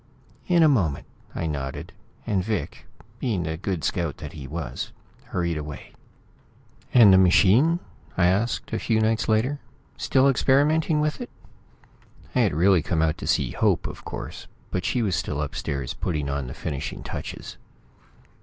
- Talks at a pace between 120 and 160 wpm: Yes, average, 155 wpm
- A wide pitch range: Yes, wide, 7.5 semitones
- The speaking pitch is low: Yes, very low, 95 Hz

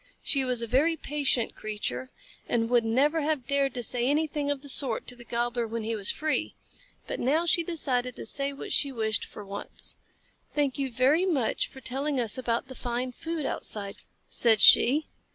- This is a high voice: Yes, very high, 255 Hz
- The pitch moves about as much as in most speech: Yes, average, 3.7 semitones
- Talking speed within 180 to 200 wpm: Yes, average, 190 wpm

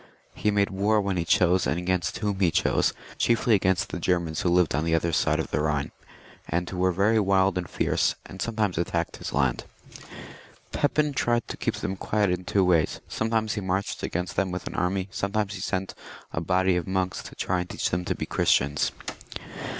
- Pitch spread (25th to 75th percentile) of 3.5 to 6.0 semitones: No, narrow, 2.4 semitones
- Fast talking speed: Yes, fast, 210 wpm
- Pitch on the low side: Yes, very low, 95 Hz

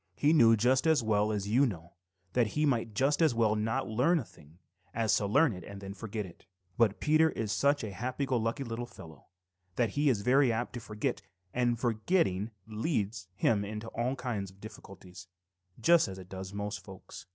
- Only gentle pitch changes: No, average, 4.1 semitones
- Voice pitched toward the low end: Yes, low, 115 Hz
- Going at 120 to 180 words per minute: No, average, 200 wpm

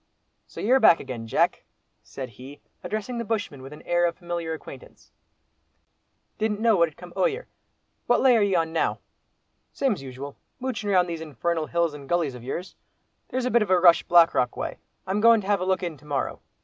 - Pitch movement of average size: No, wide, 5.9 semitones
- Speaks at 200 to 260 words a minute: Yes, fast, 205 wpm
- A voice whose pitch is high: No, medium, 175 Hz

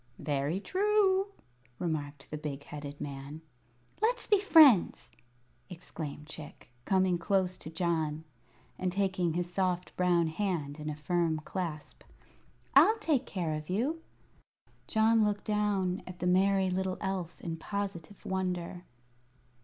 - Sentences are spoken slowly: Yes, slow, 130 wpm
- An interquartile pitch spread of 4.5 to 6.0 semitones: No, average, 4.1 semitones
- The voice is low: No, medium, 180 Hz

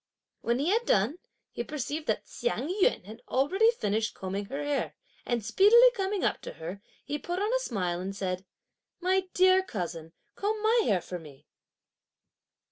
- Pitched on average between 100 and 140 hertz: No, very high, 280 Hz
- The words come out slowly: No, average, 170 wpm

